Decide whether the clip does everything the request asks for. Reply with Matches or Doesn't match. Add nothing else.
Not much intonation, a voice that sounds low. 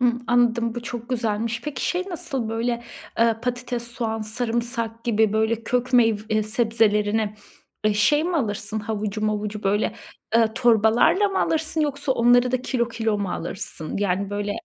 Doesn't match